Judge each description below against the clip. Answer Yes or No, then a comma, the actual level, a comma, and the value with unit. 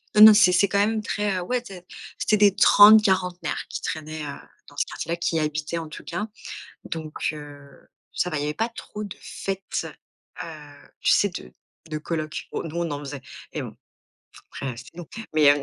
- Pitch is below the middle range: No, medium, 170 Hz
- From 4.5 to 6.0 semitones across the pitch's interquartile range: Yes, average, 5.1 semitones